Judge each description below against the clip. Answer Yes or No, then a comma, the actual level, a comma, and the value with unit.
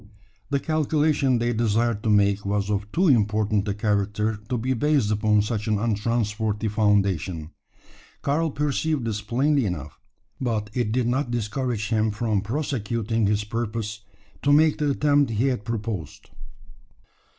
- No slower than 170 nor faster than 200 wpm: No, average, 145 wpm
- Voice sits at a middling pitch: No, low, 110 Hz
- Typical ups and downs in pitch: Yes, average, 3.8 semitones